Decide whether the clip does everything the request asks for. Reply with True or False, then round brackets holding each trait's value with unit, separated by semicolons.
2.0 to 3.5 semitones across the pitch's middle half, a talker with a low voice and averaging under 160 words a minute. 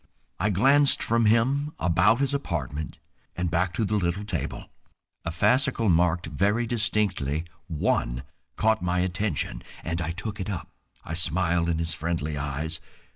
False (4.8 semitones; 90 Hz; 150 wpm)